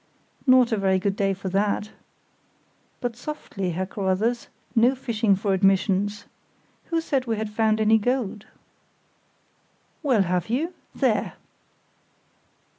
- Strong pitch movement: No, average, 3.8 semitones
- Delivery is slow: Yes, slow, 120 wpm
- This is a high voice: Yes, high, 215 Hz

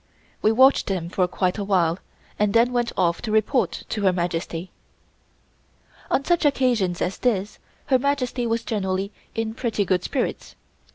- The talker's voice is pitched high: Yes, high, 210 Hz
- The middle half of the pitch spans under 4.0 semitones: No, average, 4.8 semitones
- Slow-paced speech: No, average, 160 wpm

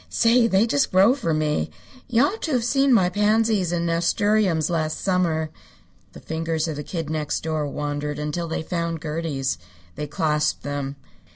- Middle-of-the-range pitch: Yes, medium, 165 Hz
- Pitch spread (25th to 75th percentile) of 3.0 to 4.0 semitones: No, average, 5.2 semitones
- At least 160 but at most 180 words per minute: Yes, average, 170 wpm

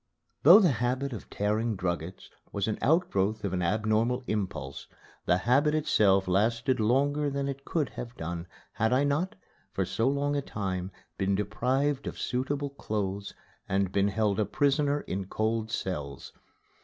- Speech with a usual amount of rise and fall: No, wide, 6.0 semitones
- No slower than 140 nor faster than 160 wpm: Yes, average, 155 wpm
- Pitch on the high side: No, low, 110 Hz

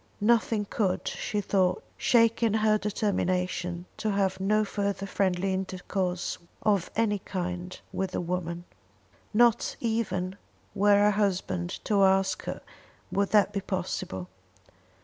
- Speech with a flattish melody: Yes, narrow, 2.3 semitones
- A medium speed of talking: No, slow, 130 wpm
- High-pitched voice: Yes, high, 195 Hz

